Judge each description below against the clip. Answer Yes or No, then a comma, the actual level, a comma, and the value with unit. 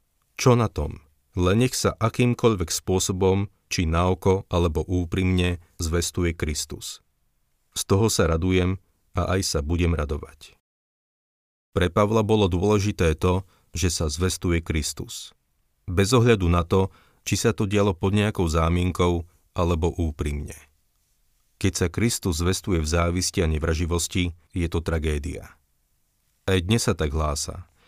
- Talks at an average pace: Yes, average, 130 wpm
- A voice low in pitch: Yes, very low, 90 Hz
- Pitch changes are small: No, average, 3.1 semitones